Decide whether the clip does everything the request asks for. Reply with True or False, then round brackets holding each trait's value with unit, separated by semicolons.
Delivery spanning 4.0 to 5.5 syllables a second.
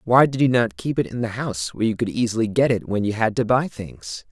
False (6.0 syllables/s)